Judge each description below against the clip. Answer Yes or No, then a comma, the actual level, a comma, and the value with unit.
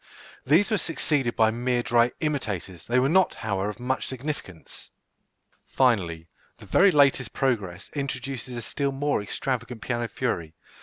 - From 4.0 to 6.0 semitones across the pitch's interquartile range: Yes, average, 4.5 semitones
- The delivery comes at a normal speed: Yes, average, 145 wpm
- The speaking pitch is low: Yes, low, 125 Hz